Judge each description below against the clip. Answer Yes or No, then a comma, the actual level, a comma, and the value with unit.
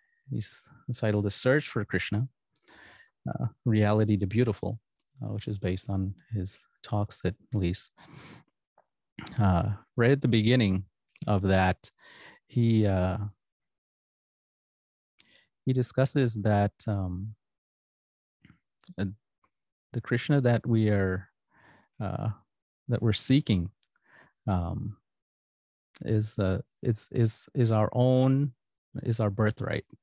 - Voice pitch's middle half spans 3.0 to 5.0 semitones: Yes, average, 3.7 semitones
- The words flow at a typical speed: No, slow, 105 wpm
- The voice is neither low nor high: No, low, 105 Hz